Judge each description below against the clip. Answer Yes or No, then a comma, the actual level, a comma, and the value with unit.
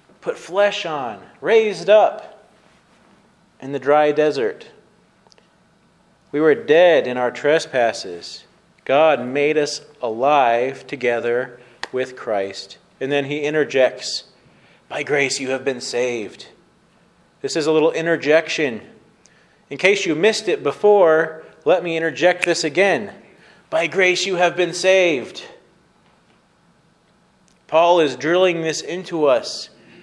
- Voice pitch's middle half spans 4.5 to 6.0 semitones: Yes, average, 5.1 semitones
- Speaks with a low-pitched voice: No, medium, 160 Hz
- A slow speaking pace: Yes, slow, 120 wpm